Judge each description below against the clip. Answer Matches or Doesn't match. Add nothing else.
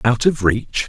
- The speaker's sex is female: Doesn't match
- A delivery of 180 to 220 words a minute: Matches